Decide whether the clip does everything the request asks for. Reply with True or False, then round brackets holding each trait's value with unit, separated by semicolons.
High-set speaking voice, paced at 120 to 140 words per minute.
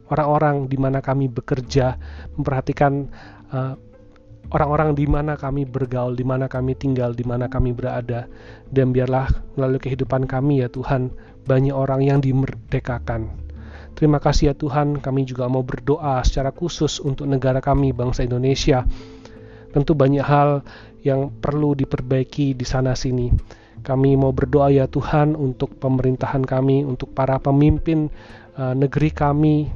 False (135 Hz; 135 wpm)